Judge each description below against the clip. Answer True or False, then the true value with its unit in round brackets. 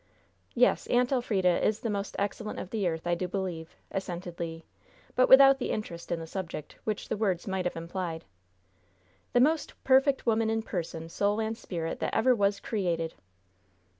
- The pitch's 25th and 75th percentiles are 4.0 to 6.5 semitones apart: True (4.6 semitones)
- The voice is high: True (195 Hz)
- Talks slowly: False (175 wpm)